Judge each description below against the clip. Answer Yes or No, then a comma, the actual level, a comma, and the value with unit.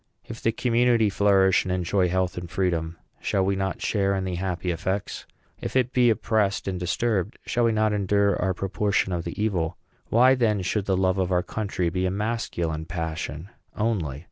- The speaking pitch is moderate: No, very low, 95 Hz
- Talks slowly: No, average, 190 wpm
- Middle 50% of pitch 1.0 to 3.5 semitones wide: Yes, average, 3.1 semitones